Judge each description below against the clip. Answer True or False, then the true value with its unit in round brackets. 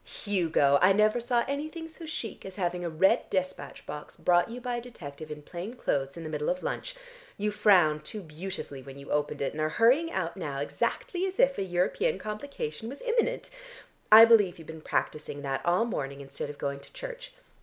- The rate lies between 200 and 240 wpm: True (205 wpm)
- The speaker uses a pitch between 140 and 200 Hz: True (190 Hz)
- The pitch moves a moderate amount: False (8.1 semitones)